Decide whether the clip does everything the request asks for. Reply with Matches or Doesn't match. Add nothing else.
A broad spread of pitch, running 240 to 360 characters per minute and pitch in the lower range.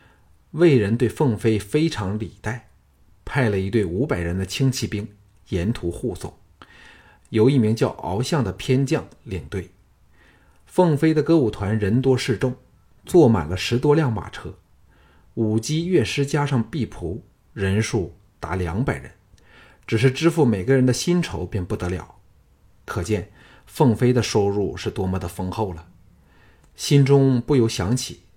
Doesn't match